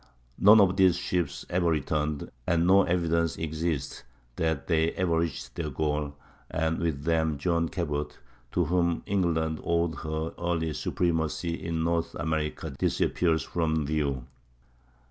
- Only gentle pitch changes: Yes, narrow, 1.9 semitones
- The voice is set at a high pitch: No, very low, 80 Hz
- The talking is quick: No, slow, 135 wpm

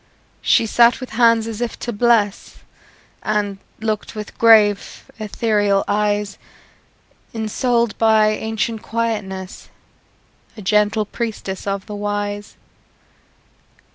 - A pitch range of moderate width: No, narrow, 1.8 semitones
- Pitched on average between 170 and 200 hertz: No, high, 215 Hz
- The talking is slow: Yes, slow, 105 wpm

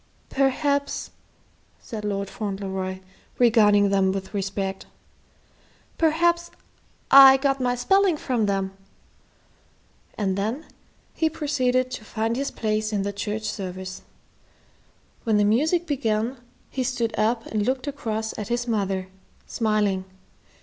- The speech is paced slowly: Yes, slow, 120 wpm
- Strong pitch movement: No, average, 4.9 semitones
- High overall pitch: Yes, high, 220 Hz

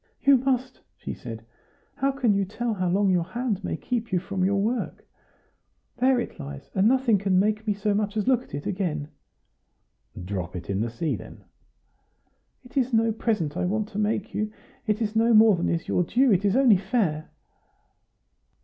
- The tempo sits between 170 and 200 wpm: Yes, average, 195 wpm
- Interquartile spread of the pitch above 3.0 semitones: Yes, average, 4.6 semitones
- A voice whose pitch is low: No, high, 205 Hz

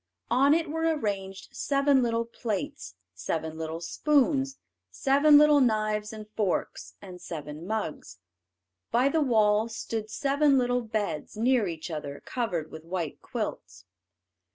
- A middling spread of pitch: No, wide, 8.0 semitones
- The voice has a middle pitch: No, high, 220 Hz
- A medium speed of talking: No, slow, 130 wpm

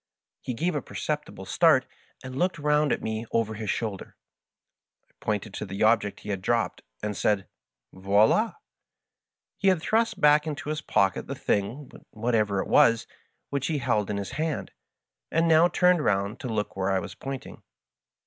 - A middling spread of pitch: No, wide, 6.5 semitones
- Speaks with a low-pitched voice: Yes, low, 115 Hz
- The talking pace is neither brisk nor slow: Yes, average, 175 wpm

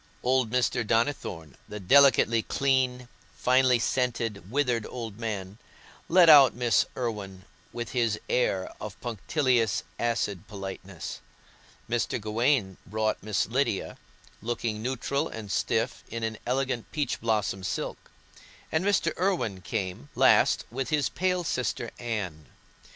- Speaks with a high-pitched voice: No, low, 115 Hz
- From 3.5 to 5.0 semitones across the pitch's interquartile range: Yes, average, 3.8 semitones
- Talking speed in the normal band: No, slow, 125 wpm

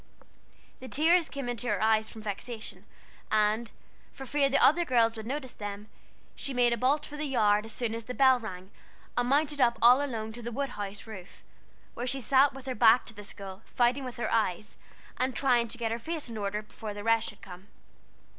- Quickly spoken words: Yes, fast, 215 wpm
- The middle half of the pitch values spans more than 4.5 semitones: No, average, 3.5 semitones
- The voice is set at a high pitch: Yes, high, 235 Hz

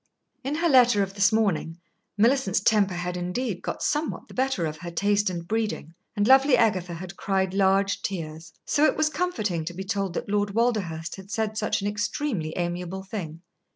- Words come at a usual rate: Yes, average, 190 wpm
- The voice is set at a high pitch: Yes, high, 195 Hz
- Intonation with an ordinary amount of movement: Yes, average, 4.0 semitones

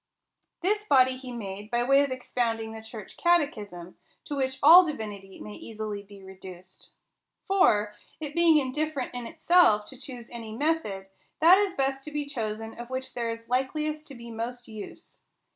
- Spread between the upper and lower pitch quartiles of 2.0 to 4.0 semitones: No, wide, 5.4 semitones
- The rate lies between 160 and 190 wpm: Yes, average, 170 wpm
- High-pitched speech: Yes, high, 245 Hz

